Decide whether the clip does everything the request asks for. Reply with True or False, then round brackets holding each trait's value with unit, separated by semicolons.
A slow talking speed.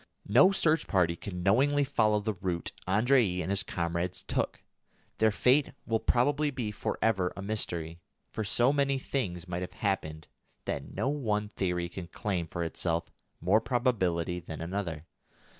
False (160 wpm)